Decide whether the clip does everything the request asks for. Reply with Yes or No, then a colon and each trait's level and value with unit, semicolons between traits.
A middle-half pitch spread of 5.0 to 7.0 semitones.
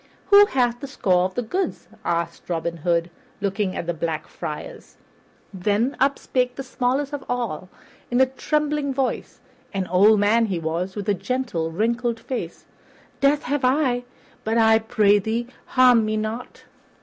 Yes: wide, 5.4 semitones